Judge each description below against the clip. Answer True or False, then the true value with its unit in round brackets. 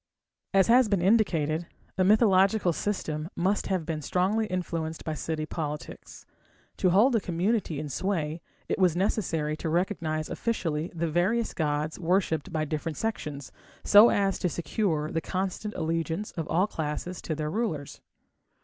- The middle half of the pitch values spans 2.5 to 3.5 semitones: False (4.1 semitones)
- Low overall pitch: False (175 Hz)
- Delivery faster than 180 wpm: False (150 wpm)